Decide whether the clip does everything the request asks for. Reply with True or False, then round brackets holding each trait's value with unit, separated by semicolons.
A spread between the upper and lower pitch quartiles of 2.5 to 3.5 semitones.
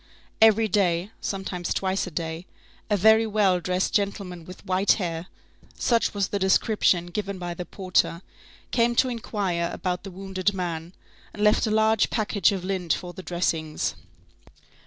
True (2.8 semitones)